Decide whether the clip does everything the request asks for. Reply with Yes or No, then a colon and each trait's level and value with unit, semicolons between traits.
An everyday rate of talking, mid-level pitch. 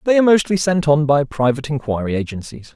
Yes: average, 195 wpm; medium, 150 Hz